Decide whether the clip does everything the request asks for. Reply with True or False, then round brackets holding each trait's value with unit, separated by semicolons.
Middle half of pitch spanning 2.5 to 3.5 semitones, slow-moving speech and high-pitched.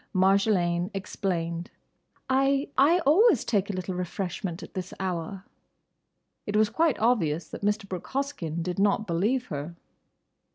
False (5.3 semitones; 130 wpm; 195 Hz)